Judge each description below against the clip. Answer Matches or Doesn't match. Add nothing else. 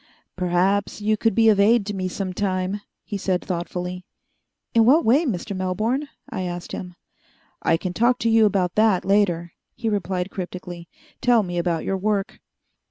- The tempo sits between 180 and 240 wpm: Doesn't match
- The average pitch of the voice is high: Matches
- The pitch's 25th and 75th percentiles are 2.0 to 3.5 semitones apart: Matches